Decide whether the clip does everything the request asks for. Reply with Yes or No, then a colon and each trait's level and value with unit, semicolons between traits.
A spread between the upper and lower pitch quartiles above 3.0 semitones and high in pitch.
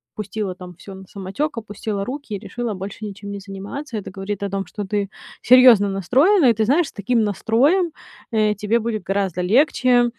Yes: average, 3.7 semitones; high, 210 Hz